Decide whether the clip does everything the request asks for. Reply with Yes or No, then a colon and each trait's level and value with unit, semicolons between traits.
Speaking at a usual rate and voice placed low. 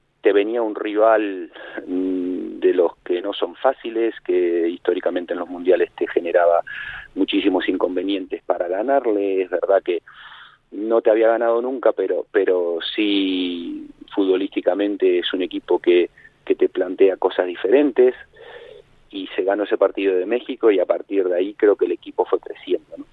No: average, 160 wpm; very high, 365 Hz